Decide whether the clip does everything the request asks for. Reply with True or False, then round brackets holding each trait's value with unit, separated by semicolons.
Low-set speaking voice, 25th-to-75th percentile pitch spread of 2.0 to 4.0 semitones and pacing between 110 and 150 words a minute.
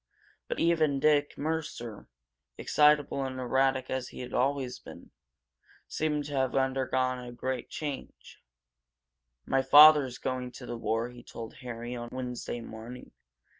True (130 Hz; 2.6 semitones; 135 wpm)